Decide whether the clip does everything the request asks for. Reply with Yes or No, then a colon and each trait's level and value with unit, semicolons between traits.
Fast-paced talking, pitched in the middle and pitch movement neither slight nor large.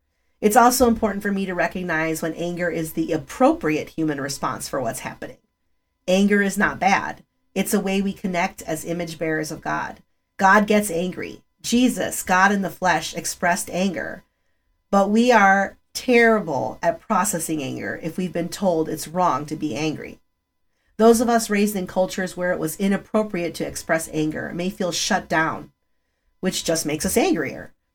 No: average, 170 wpm; medium, 180 Hz; average, 3.8 semitones